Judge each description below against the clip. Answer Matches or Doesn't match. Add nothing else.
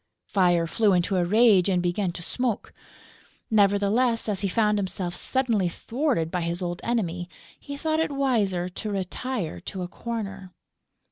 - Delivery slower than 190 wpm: Matches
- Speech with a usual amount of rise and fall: Matches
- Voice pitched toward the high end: Matches